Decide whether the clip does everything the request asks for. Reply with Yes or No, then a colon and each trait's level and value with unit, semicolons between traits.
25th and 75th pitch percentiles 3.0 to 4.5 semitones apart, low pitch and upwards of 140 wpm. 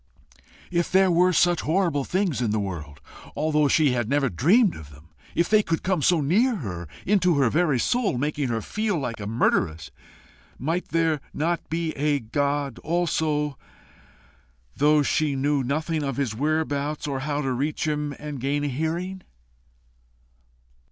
No: average, 4.0 semitones; medium, 150 Hz; average, 160 wpm